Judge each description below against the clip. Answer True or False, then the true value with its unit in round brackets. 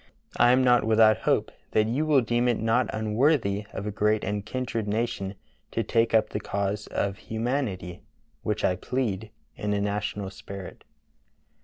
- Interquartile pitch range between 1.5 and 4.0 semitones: True (2.8 semitones)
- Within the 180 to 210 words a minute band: False (165 wpm)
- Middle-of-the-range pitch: False (110 Hz)